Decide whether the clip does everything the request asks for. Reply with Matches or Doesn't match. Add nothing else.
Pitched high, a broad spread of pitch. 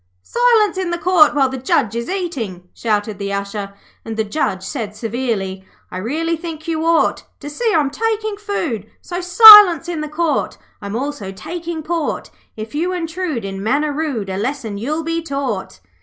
Matches